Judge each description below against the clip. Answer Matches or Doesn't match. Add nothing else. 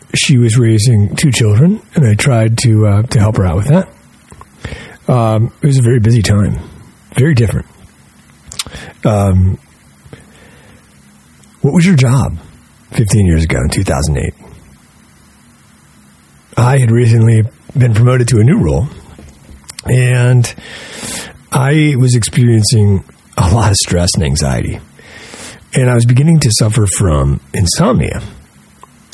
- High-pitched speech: Doesn't match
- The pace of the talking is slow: Matches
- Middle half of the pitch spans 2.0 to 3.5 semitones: Doesn't match